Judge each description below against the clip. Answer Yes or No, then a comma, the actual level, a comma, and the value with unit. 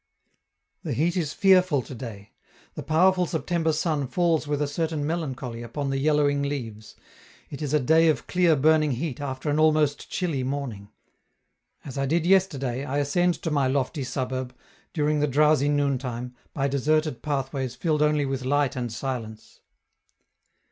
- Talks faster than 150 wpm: Yes, average, 160 wpm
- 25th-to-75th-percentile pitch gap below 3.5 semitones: Yes, average, 3.1 semitones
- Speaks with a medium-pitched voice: Yes, medium, 145 Hz